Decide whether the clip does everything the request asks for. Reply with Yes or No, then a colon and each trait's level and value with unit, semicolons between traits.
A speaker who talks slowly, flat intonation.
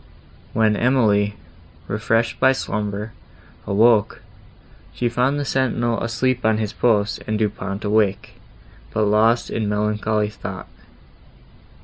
Yes: slow, 115 wpm; narrow, 2.1 semitones